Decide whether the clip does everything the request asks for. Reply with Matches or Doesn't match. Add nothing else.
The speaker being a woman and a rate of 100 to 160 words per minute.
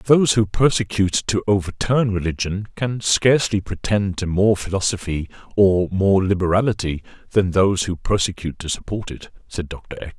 Doesn't match